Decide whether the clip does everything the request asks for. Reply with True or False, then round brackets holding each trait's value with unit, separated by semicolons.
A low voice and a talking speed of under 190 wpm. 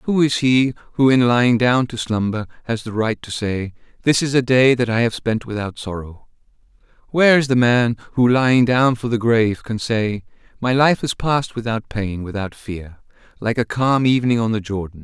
False (115 Hz; 205 wpm)